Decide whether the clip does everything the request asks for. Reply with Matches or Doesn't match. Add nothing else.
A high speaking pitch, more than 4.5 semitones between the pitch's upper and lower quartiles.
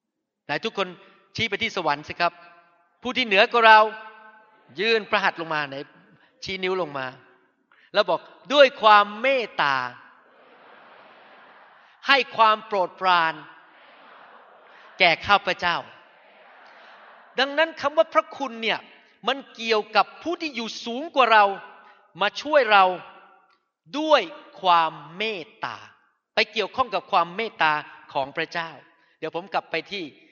Matches